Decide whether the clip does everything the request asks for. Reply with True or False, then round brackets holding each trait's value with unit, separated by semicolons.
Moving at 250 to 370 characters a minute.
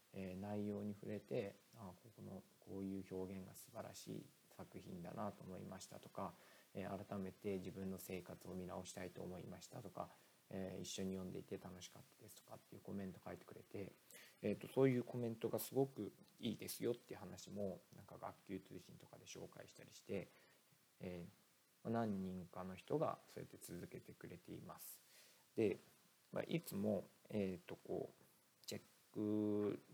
True (335 characters per minute)